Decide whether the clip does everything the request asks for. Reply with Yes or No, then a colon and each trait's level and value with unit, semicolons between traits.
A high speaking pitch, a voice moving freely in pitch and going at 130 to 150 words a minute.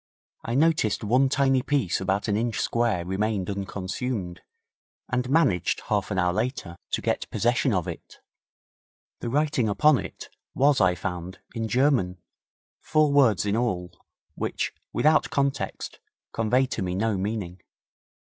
No: low, 110 Hz; wide, 5.7 semitones; average, 140 wpm